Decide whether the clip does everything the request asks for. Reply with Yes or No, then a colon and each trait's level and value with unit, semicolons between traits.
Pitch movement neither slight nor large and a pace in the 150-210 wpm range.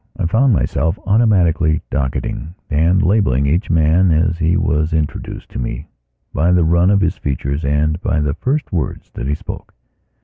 Yes: average, 3.6 semitones; average, 170 wpm